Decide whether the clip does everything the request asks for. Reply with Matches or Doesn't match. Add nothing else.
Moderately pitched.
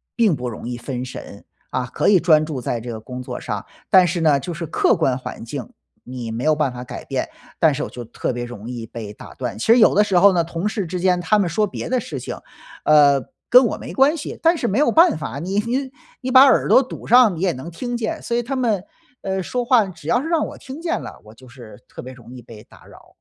Matches